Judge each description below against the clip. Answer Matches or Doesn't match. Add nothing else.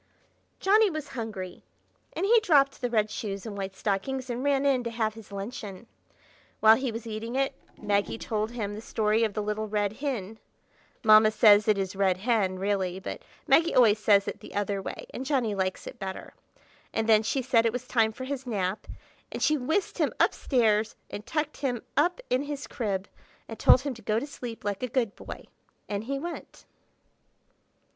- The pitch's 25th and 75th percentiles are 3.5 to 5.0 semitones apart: Matches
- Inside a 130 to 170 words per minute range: Doesn't match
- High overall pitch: Matches